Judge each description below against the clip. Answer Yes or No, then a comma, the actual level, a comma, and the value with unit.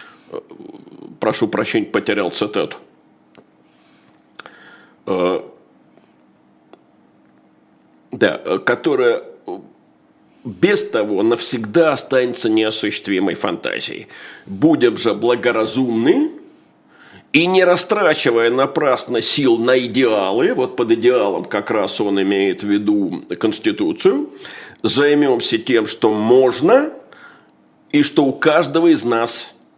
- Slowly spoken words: Yes, slow, 85 wpm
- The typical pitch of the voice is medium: Yes, medium, 170 Hz